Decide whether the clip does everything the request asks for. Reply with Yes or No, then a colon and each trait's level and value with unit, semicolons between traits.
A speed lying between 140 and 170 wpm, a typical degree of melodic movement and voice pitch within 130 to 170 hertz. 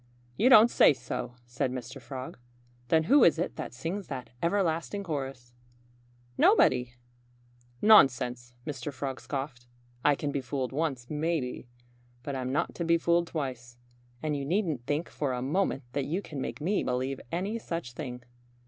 Yes: average, 160 wpm; average, 4.8 semitones; medium, 140 Hz